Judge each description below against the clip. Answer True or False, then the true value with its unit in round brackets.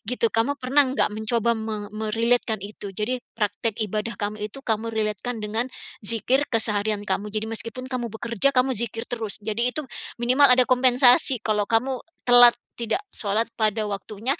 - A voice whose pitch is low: False (225 Hz)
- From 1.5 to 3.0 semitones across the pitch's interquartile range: True (2.6 semitones)